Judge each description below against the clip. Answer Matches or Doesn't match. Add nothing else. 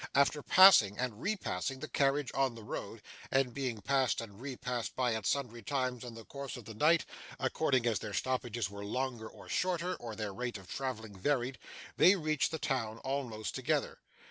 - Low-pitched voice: Matches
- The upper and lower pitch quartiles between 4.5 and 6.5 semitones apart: Doesn't match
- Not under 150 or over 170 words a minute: Doesn't match